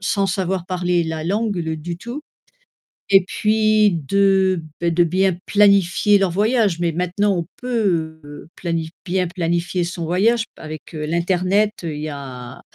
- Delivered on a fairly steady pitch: No, average, 3.1 semitones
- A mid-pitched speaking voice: Yes, medium, 180 Hz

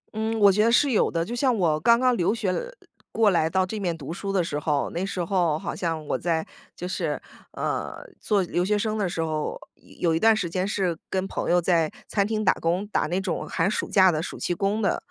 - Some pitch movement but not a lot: Yes, average, 4.0 semitones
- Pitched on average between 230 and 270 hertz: No, medium, 185 Hz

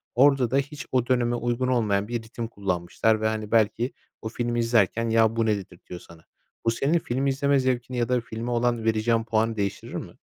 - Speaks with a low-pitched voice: Yes, low, 115 Hz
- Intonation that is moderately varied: No, narrow, 2.0 semitones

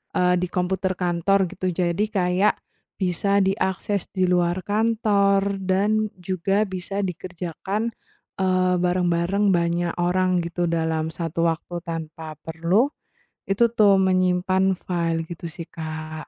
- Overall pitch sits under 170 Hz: No, medium, 180 Hz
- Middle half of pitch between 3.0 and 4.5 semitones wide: No, narrow, 2.4 semitones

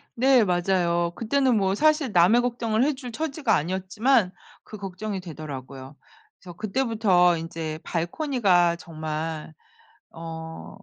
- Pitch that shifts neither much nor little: No, wide, 6.0 semitones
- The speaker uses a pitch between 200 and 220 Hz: No, high, 190 Hz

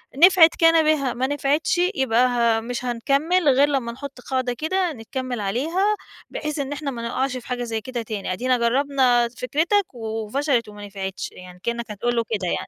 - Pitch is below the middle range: No, very high, 250 Hz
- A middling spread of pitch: Yes, average, 3.8 semitones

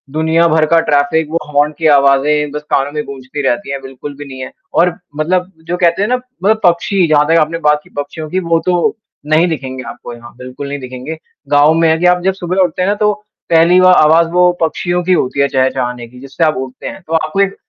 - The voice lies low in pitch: No, medium, 155 Hz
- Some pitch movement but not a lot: Yes, average, 4.1 semitones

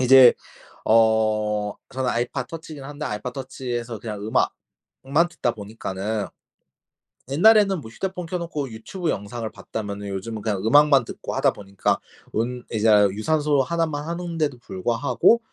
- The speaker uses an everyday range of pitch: No, wide, 5.7 semitones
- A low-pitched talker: Yes, low, 125 Hz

